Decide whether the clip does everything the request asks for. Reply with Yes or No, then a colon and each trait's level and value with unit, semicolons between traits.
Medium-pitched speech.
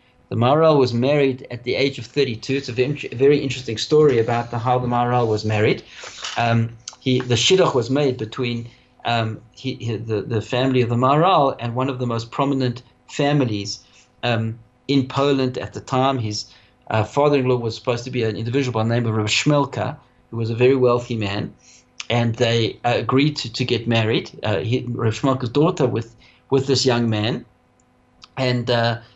No: low, 125 Hz